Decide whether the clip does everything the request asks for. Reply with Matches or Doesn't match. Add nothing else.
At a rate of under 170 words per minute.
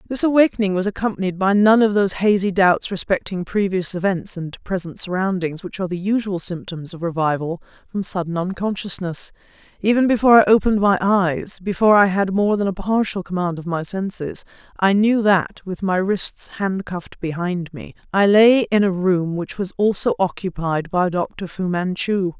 Doesn't match